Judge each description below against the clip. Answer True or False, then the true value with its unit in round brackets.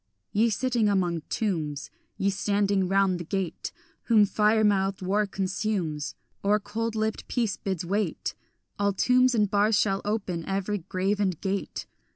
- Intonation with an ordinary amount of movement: False (2.0 semitones)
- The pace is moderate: True (150 wpm)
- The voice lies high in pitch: True (200 Hz)